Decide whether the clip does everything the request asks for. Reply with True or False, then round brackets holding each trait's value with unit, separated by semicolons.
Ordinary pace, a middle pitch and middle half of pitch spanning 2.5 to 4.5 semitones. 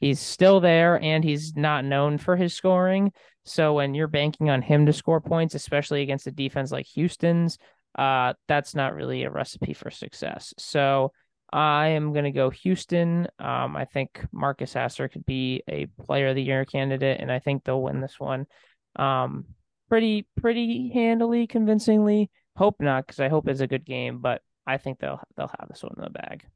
True (190 wpm; 145 Hz; 4.2 semitones)